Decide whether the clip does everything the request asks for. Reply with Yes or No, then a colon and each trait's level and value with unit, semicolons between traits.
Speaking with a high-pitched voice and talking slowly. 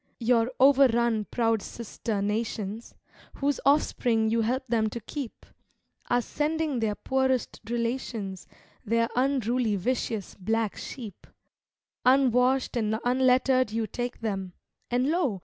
Yes: high, 235 Hz; slow, 115 wpm